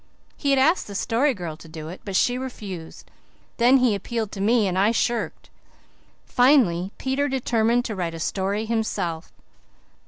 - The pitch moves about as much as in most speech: Yes, average, 5.0 semitones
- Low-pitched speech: No, high, 220 Hz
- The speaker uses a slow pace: No, average, 165 wpm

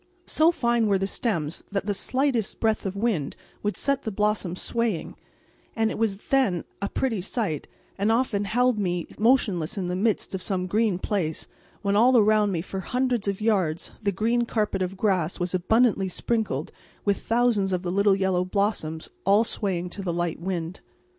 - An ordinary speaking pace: Yes, average, 180 wpm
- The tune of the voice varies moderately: Yes, average, 3.6 semitones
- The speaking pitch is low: No, high, 200 Hz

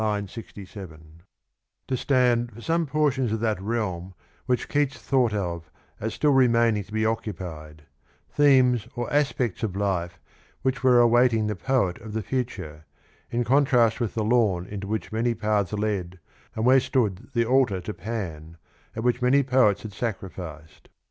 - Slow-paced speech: No, average, 155 wpm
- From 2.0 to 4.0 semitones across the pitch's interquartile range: No, average, 4.5 semitones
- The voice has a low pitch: Yes, low, 110 Hz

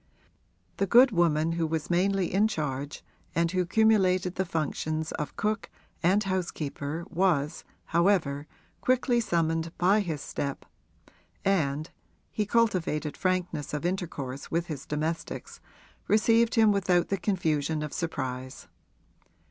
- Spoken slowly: Yes, slow, 125 wpm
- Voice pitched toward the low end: No, medium, 170 Hz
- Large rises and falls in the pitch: No, average, 4.2 semitones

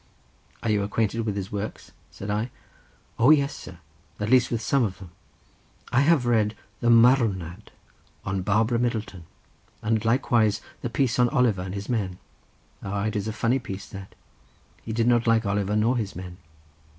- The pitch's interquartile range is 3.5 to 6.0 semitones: No, average, 3.1 semitones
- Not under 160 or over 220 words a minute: Yes, average, 170 wpm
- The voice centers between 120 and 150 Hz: No, low, 110 Hz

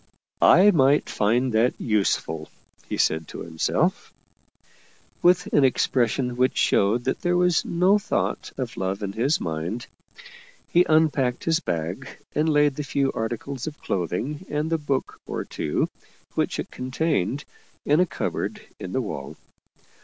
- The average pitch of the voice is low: Yes, low, 130 Hz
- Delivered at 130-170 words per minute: Yes, average, 155 wpm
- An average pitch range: No, wide, 6.9 semitones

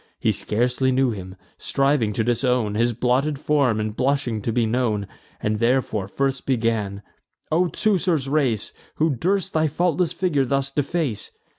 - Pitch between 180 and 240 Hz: No, low, 130 Hz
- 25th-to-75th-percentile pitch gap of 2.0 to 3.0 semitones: No, average, 4.5 semitones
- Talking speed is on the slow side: No, average, 150 wpm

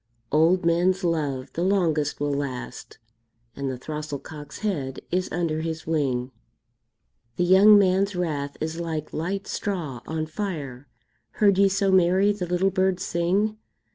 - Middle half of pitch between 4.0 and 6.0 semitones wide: Yes, average, 4.3 semitones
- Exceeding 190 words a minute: No, average, 145 wpm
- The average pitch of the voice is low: No, medium, 170 Hz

